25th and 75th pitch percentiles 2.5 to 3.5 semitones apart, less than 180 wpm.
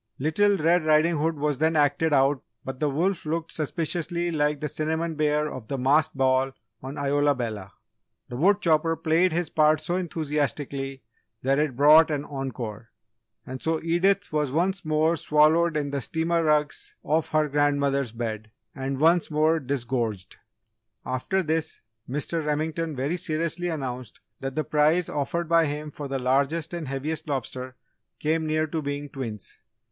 Yes: average, 2.9 semitones; average, 160 wpm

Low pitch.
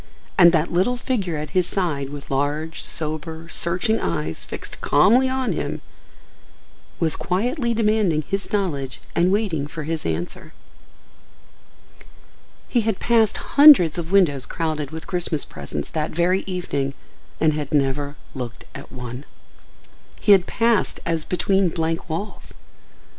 No: medium, 165 Hz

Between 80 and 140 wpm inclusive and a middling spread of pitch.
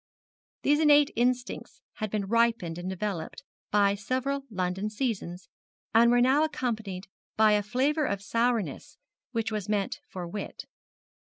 Yes: slow, 135 wpm; average, 4.1 semitones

